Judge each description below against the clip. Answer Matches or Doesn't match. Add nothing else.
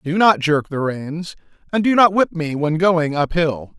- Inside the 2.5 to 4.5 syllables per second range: Matches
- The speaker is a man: Matches